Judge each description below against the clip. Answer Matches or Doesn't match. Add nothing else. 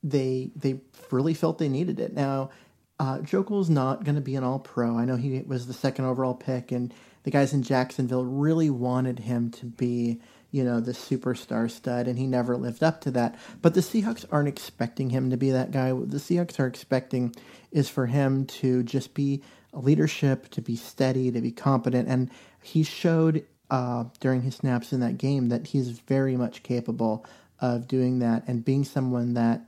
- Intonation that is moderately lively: Doesn't match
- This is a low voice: Matches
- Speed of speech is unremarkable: Matches